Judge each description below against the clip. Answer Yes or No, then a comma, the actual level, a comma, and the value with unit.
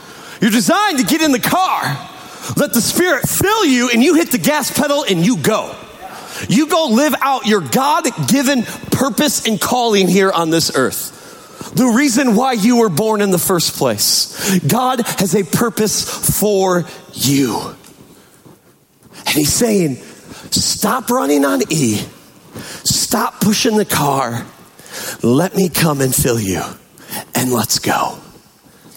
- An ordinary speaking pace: Yes, average, 145 wpm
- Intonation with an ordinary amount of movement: No, wide, 7.4 semitones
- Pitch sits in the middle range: No, high, 215 Hz